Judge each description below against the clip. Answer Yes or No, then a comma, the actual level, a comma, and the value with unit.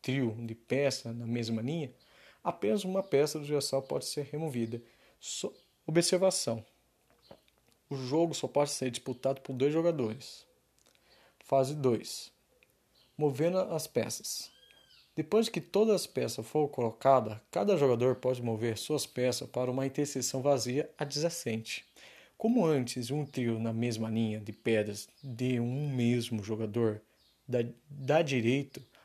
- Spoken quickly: No, average, 130 wpm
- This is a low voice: Yes, low, 130 Hz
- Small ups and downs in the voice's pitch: No, average, 4.0 semitones